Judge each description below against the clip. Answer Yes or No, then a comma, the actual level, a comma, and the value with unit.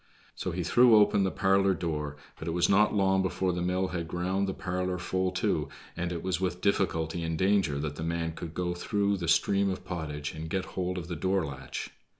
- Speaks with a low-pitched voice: Yes, very low, 90 Hz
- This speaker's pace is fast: Yes, fast, 220 wpm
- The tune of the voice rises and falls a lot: No, narrow, 2.5 semitones